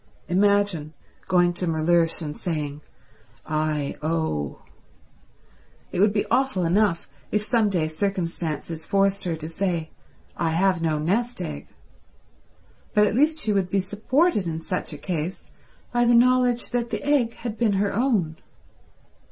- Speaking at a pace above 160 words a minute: No, average, 145 wpm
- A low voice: No, medium, 185 Hz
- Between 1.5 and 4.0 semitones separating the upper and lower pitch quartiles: No, average, 4.8 semitones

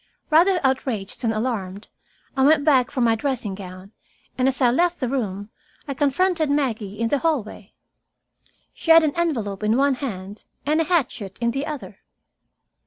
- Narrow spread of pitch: No, wide, 5.6 semitones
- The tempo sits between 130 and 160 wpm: No, average, 170 wpm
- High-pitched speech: Yes, very high, 255 Hz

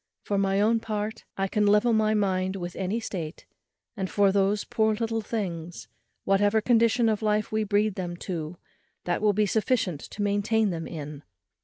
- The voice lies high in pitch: Yes, high, 205 Hz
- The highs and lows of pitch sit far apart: No, narrow, 2.6 semitones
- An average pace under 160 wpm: No, average, 175 wpm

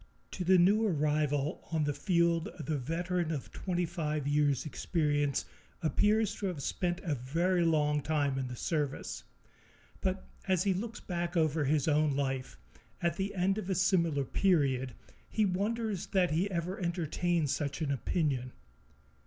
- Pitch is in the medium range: Yes, medium, 165 Hz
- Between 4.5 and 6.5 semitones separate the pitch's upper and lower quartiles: No, average, 4.0 semitones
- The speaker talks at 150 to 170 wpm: Yes, average, 155 wpm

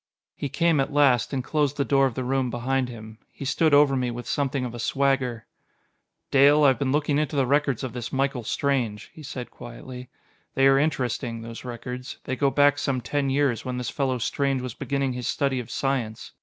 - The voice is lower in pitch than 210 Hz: Yes, low, 135 Hz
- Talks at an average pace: No, fast, 210 wpm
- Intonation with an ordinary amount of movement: No, narrow, 2.2 semitones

